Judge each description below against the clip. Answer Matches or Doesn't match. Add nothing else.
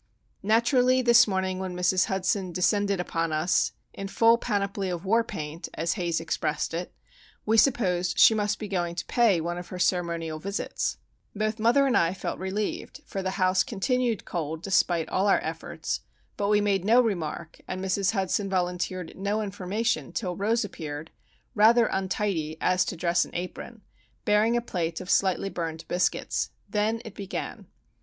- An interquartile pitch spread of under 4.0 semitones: Matches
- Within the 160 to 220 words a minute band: Matches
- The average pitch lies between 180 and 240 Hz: Matches